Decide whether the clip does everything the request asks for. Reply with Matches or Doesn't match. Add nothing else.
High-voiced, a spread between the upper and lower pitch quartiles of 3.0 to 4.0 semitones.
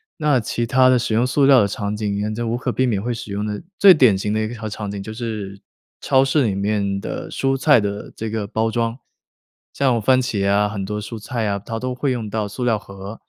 Doesn't match